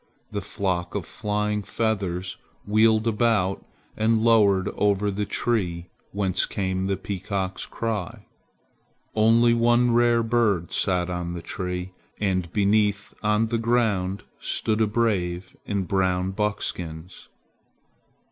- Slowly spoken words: Yes, slow, 120 wpm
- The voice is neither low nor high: No, low, 100 Hz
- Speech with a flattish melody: No, average, 3.1 semitones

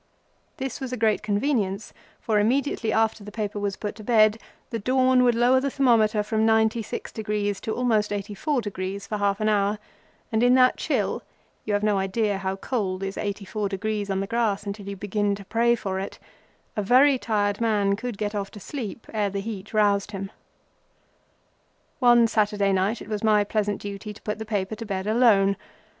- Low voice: No, high, 210 Hz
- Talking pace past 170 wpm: Yes, average, 180 wpm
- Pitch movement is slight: Yes, narrow, 2.2 semitones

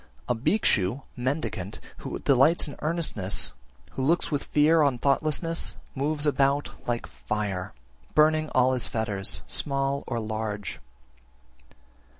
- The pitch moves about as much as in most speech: No, wide, 5.7 semitones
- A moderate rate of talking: No, slow, 125 wpm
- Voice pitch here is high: No, low, 135 Hz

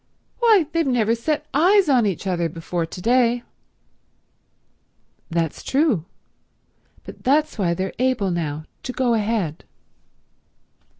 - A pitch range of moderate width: No, wide, 8.0 semitones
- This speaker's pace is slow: Yes, slow, 120 wpm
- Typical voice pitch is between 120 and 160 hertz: No, high, 230 Hz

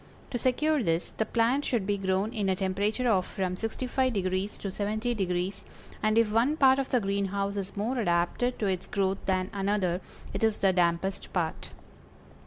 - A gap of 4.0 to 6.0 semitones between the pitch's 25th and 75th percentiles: No, average, 3.4 semitones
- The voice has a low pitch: No, high, 200 Hz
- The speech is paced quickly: No, average, 175 wpm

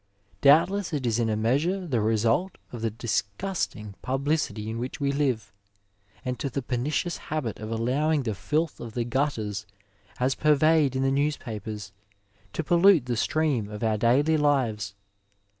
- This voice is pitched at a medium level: No, low, 130 Hz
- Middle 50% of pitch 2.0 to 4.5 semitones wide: No, average, 5.3 semitones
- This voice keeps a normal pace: Yes, average, 160 wpm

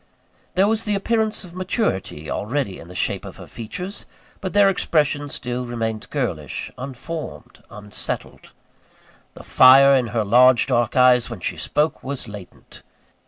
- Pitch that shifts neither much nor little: No, wide, 7.6 semitones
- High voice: No, low, 130 Hz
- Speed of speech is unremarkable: Yes, average, 150 wpm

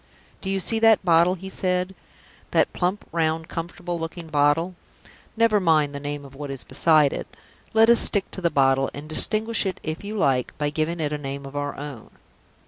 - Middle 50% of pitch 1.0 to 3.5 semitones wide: No, average, 4.4 semitones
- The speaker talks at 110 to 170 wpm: No, average, 200 wpm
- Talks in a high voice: No, medium, 165 Hz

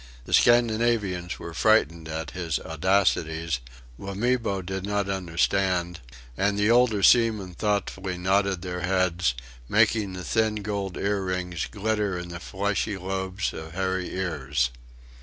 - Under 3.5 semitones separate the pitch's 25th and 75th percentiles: Yes, average, 2.7 semitones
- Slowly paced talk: Yes, slow, 125 wpm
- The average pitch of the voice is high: No, very low, 95 Hz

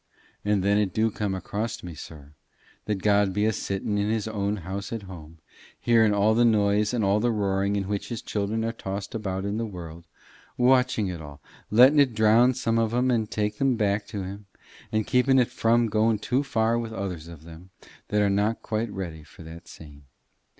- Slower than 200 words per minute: No, fast, 205 wpm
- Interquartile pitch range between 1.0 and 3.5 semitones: Yes, average, 2.8 semitones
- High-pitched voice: No, low, 105 Hz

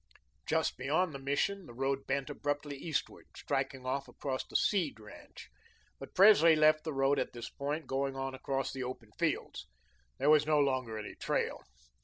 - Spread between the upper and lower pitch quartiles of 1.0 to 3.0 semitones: Yes, narrow, 2.4 semitones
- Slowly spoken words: No, average, 175 wpm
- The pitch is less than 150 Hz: Yes, medium, 140 Hz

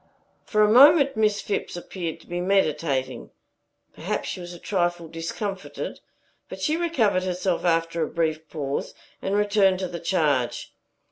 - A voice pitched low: No, medium, 180 Hz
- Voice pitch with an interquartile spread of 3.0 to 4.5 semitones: Yes, average, 3.8 semitones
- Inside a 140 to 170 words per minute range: Yes, average, 150 wpm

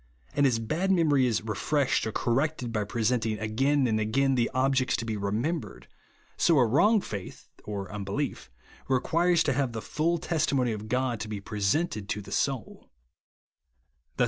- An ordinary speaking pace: Yes, average, 160 wpm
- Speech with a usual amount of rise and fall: Yes, average, 4.8 semitones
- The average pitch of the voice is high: No, low, 125 Hz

